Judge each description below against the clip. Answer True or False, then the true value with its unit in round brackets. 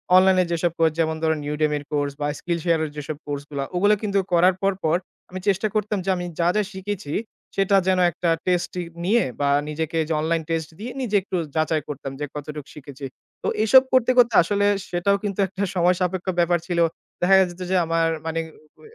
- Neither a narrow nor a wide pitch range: True (3.6 semitones)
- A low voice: False (175 Hz)